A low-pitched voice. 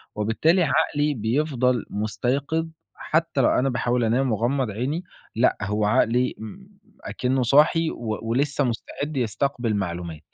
Yes: low, 125 Hz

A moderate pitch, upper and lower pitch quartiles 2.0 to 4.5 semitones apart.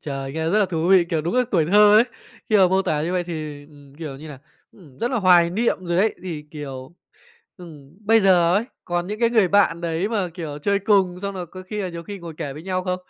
Yes: medium, 175 Hz; average, 4.0 semitones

